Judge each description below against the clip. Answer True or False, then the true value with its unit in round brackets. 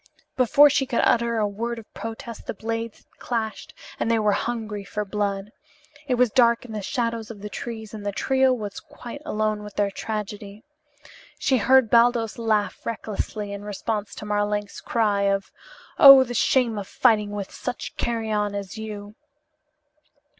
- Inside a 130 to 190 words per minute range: True (170 wpm)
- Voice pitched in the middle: False (220 Hz)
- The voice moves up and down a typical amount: False (2.2 semitones)